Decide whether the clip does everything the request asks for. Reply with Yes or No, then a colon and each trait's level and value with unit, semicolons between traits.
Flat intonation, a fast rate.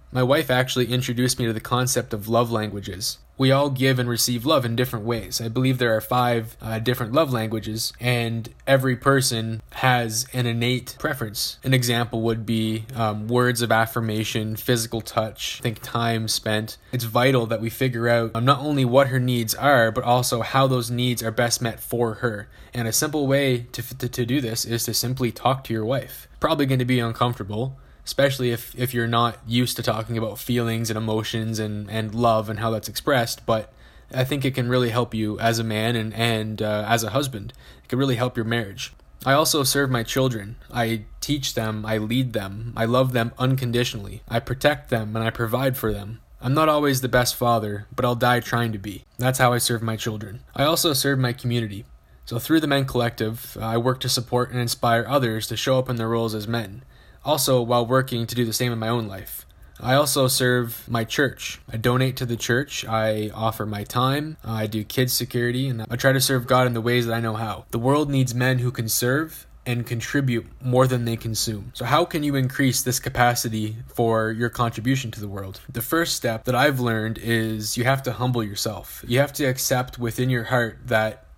Yes: narrow, 2.1 semitones; fast, 215 wpm